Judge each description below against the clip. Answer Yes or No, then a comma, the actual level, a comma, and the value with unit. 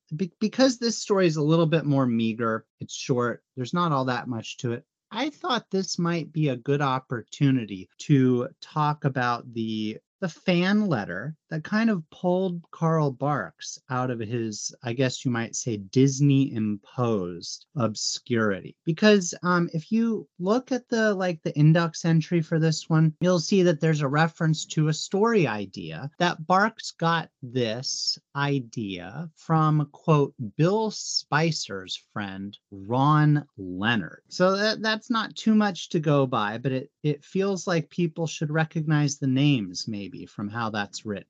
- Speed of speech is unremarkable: Yes, average, 160 wpm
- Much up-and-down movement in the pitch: Yes, wide, 6.0 semitones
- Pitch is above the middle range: No, medium, 155 Hz